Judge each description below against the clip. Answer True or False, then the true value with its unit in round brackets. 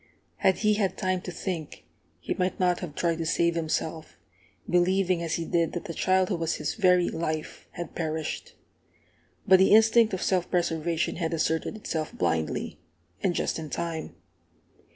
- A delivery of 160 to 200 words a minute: True (170 wpm)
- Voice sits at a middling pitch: True (175 Hz)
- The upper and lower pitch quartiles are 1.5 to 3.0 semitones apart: True (2.4 semitones)